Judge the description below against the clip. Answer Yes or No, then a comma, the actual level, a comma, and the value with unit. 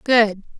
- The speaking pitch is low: No, high, 220 Hz